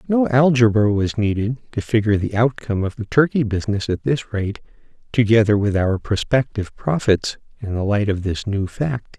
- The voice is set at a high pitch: No, low, 110 Hz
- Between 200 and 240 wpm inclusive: No, average, 175 wpm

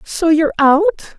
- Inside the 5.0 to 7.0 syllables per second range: Yes, 5.8 syllables/s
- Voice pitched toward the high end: Yes, very high, 305 Hz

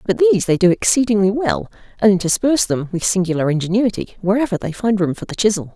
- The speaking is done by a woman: Yes, female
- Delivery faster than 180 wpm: Yes, average, 200 wpm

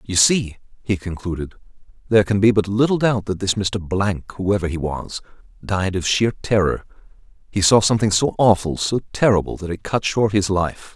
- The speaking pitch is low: Yes, low, 100 Hz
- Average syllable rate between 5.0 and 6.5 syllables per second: Yes, 5.2 syllables/s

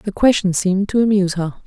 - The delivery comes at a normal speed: No, fast, 215 wpm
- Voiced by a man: No, female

